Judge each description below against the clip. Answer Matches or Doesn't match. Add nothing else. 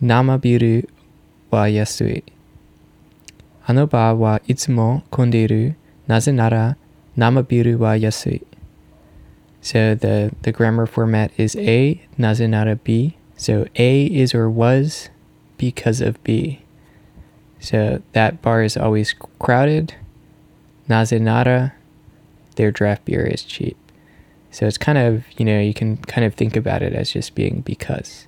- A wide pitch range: Doesn't match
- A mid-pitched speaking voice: Doesn't match